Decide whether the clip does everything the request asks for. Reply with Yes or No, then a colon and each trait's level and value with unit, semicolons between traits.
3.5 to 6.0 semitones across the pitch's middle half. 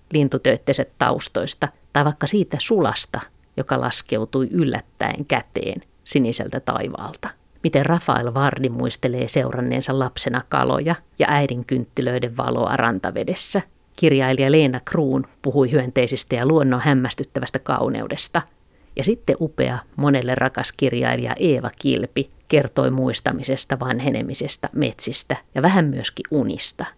No: narrow, 2.6 semitones